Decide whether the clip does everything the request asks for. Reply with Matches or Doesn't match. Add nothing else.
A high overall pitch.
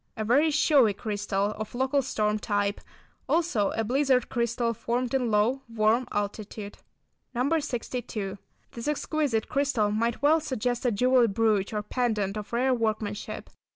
Matches